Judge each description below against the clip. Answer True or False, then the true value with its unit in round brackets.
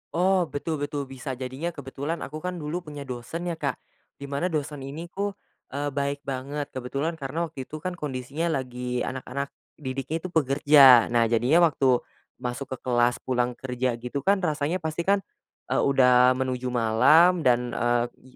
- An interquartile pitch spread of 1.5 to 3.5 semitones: False (3.9 semitones)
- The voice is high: False (140 Hz)